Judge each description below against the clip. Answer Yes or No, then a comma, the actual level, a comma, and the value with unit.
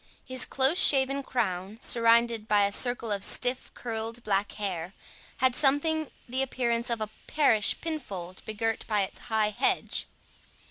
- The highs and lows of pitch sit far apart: No, average, 3.8 semitones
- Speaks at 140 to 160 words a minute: Yes, average, 145 wpm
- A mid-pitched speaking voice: No, high, 230 Hz